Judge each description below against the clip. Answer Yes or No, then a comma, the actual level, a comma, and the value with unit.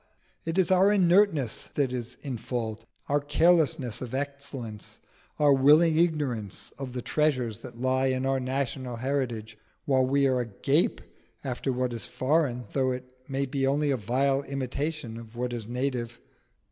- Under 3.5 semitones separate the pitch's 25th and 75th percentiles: Yes, average, 2.7 semitones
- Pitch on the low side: Yes, low, 130 Hz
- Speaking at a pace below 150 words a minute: No, average, 160 wpm